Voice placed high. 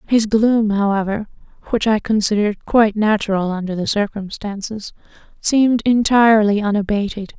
Yes: high, 210 Hz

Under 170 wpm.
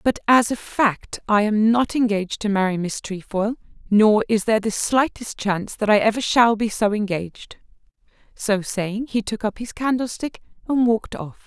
No: average, 185 wpm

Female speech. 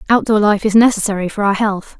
Yes: female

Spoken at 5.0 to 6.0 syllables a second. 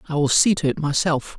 Yes: 5.8 syllables/s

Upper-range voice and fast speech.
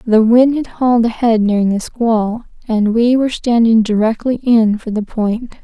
No: high, 230 Hz; average, 180 wpm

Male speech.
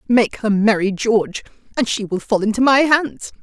No: female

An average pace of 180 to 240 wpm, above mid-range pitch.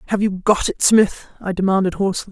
Yes: fast, 205 wpm; high, 195 Hz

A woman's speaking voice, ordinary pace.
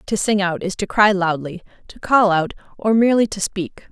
No: female; fast, 215 wpm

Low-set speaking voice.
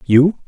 No: medium, 155 Hz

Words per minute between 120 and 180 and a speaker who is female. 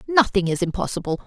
Yes: average, 140 wpm; female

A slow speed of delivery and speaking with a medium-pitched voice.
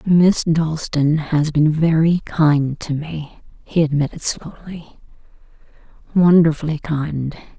Yes: slow, 105 wpm; medium, 155 Hz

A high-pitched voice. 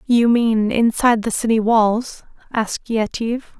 Yes: high, 225 Hz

